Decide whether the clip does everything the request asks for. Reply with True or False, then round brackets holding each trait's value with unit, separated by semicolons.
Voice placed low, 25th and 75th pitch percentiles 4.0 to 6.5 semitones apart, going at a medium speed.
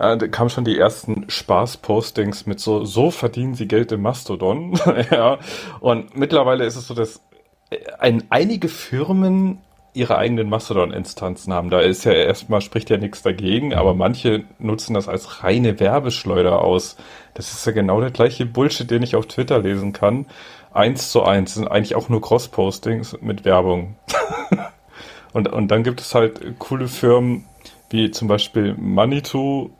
False (115 Hz; 3.1 semitones; 160 wpm)